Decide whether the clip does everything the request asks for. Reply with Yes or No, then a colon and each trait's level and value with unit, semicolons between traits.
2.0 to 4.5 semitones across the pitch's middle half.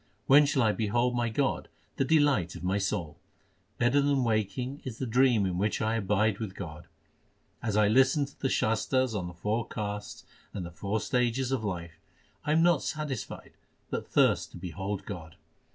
No: average, 5.0 semitones